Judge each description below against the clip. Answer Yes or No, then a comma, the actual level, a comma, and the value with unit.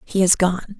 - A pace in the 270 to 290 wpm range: No, fast, 225 wpm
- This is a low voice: No, high, 190 Hz